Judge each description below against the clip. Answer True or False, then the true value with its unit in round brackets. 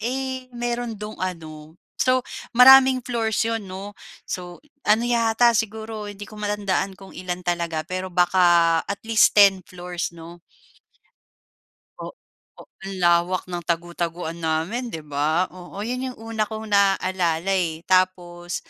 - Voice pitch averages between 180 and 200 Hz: True (190 Hz)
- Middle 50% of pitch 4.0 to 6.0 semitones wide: True (4.3 semitones)